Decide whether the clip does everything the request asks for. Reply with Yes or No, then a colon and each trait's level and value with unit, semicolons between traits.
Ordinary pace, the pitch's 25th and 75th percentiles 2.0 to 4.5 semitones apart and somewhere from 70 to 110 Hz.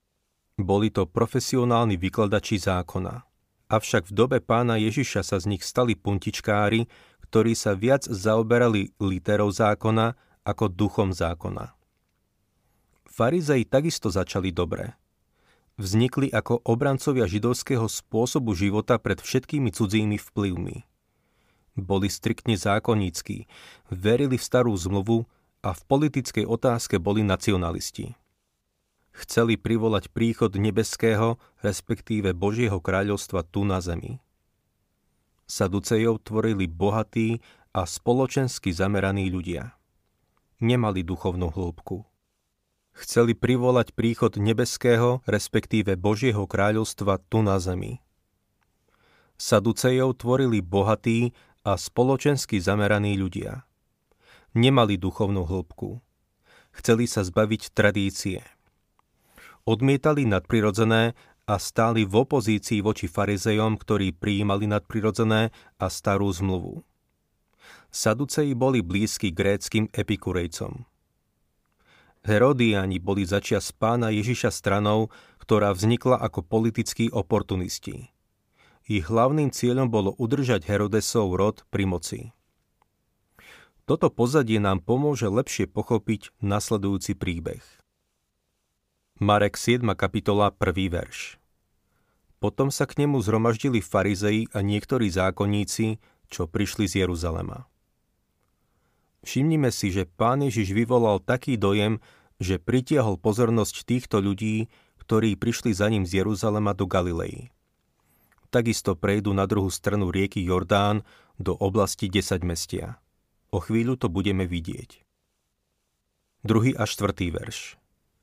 No: slow, 105 wpm; average, 2.9 semitones; low, 105 Hz